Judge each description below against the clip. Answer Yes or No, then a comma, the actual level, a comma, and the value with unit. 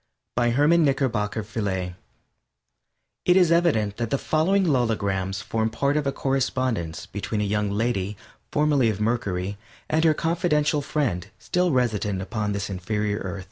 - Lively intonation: Yes, wide, 6.2 semitones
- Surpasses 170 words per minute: No, average, 150 wpm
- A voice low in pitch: Yes, low, 115 Hz